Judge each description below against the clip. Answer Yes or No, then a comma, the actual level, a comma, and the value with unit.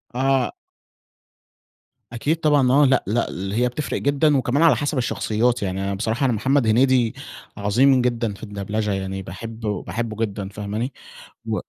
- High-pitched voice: No, low, 115 Hz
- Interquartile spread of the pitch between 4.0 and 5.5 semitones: Yes, average, 4.3 semitones